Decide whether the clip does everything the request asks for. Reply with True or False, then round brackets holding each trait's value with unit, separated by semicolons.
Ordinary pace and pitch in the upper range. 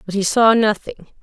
True (195 wpm; 210 Hz)